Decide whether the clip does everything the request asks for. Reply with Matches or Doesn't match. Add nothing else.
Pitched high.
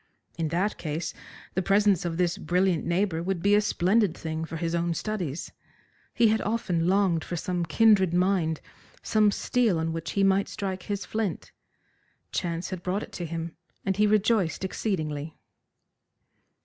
Doesn't match